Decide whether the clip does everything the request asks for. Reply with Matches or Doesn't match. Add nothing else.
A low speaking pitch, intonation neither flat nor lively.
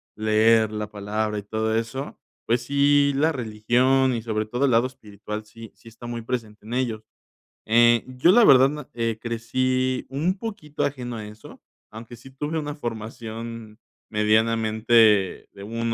Matches